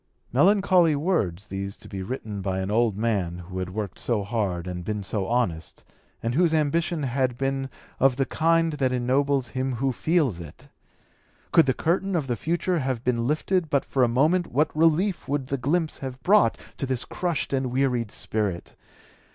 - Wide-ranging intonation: Yes, wide, 6.5 semitones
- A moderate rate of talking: Yes, average, 185 wpm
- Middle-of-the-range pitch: No, low, 130 Hz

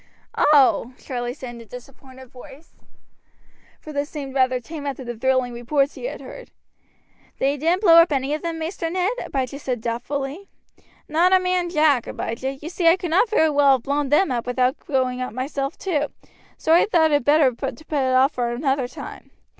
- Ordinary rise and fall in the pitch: Yes, average, 3.8 semitones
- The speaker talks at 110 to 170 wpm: No, average, 200 wpm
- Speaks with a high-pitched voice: Yes, very high, 280 Hz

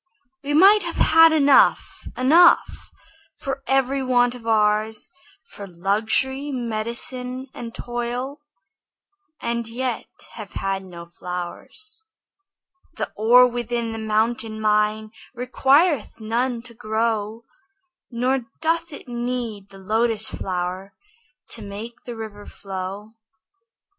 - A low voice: No, high, 235 Hz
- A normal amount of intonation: Yes, average, 3.4 semitones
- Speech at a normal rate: No, slow, 110 wpm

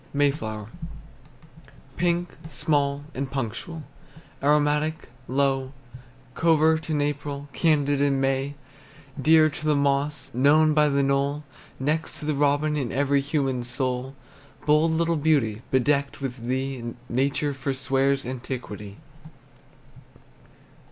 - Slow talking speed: Yes, slow, 110 wpm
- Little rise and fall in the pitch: Yes, narrow, 2.1 semitones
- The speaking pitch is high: No, medium, 140 Hz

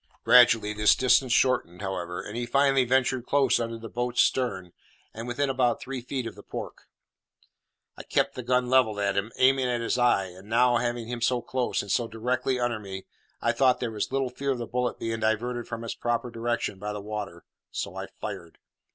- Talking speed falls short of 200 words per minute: No, fast, 205 wpm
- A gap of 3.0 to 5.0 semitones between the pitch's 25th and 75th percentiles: No, narrow, 2.6 semitones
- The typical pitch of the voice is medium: No, low, 120 Hz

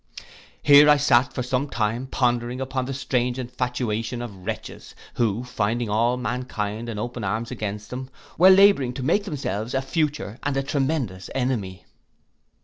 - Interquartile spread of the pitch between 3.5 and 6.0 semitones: No, average, 3.1 semitones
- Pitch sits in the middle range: No, low, 125 Hz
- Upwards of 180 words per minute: No, average, 155 wpm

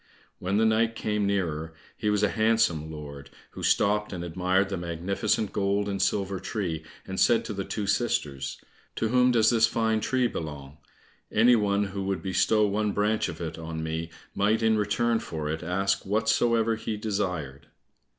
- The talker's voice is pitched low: Yes, low, 100 Hz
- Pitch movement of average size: Yes, average, 4.2 semitones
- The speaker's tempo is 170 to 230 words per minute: Yes, average, 175 wpm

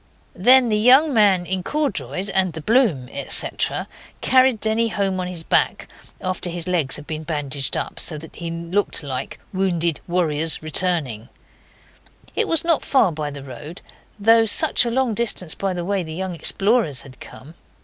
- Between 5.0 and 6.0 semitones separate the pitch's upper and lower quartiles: Yes, wide, 5.6 semitones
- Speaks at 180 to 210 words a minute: No, average, 170 wpm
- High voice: No, medium, 180 Hz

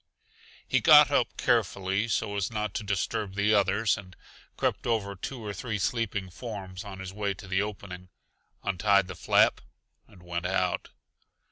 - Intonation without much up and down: Yes, narrow, 2.0 semitones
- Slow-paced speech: No, average, 160 wpm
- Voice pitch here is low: Yes, low, 100 Hz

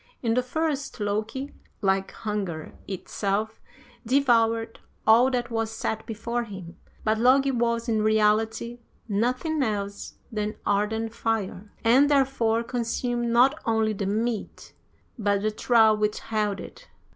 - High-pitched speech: Yes, high, 225 Hz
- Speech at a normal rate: No, slow, 130 wpm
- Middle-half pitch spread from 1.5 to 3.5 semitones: Yes, narrow, 2.4 semitones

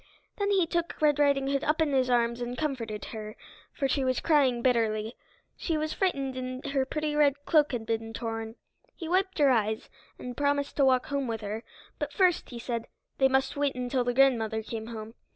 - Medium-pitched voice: No, very high, 265 Hz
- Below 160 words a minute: No, fast, 205 wpm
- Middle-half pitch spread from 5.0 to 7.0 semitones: No, average, 4.0 semitones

